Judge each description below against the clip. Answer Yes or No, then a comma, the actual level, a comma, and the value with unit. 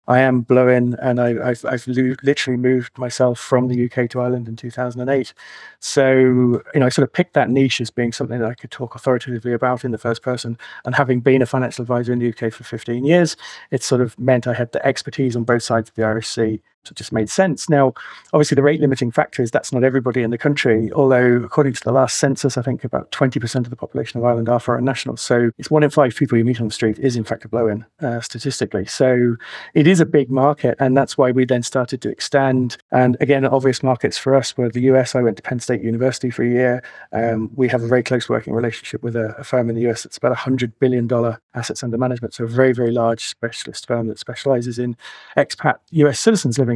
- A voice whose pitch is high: No, low, 125 Hz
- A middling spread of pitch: No, narrow, 2.1 semitones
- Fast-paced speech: Yes, fast, 240 wpm